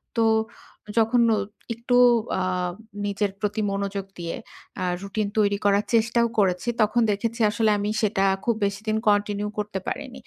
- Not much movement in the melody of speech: Yes, narrow, 2.2 semitones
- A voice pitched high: Yes, high, 210 Hz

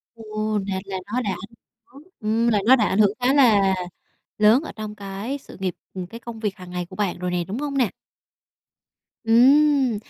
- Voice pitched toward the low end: No, high, 215 Hz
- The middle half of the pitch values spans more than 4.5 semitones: No, average, 4.0 semitones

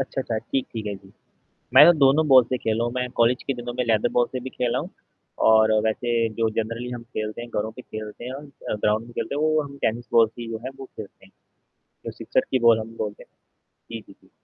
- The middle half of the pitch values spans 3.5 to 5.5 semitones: No, narrow, 2.5 semitones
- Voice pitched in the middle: No, low, 120 Hz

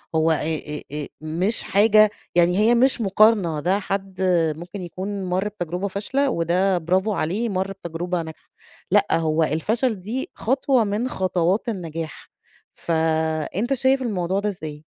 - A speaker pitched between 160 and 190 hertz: Yes, medium, 185 Hz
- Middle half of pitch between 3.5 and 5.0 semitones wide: Yes, average, 4.3 semitones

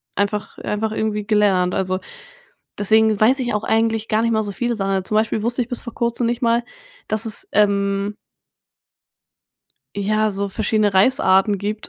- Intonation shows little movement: Yes, narrow, 1.9 semitones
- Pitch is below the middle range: No, high, 215 Hz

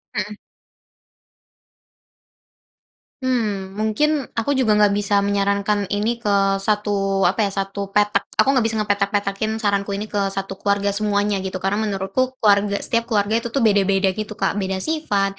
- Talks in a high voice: Yes, high, 205 Hz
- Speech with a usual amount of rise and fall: No, narrow, 1.4 semitones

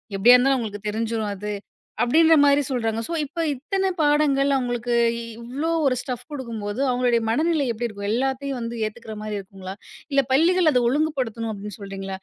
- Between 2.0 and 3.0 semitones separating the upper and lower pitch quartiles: No, average, 4.6 semitones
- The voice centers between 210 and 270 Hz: Yes, high, 245 Hz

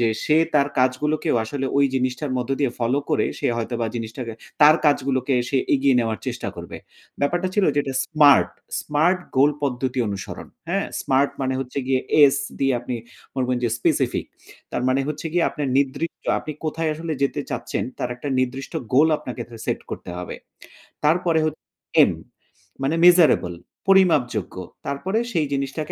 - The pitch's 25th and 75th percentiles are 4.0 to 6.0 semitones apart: No, average, 3.2 semitones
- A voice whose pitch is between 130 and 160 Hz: Yes, medium, 140 Hz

